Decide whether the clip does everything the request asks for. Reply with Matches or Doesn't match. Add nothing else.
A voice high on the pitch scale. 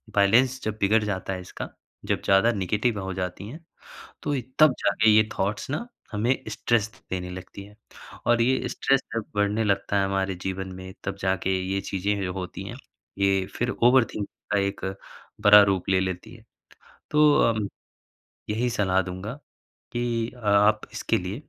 Doesn't match